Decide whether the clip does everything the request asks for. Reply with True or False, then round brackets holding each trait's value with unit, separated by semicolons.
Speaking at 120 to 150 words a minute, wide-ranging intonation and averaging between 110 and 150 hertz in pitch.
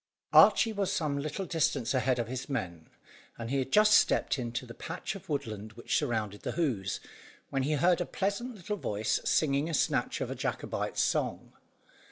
False (185 wpm; 6.9 semitones; 140 Hz)